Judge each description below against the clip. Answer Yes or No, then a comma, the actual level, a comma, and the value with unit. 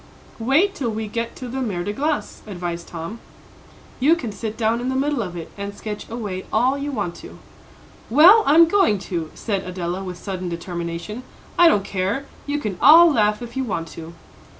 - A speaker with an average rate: Yes, average, 195 wpm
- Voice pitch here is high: Yes, high, 215 Hz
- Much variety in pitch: Yes, wide, 6.4 semitones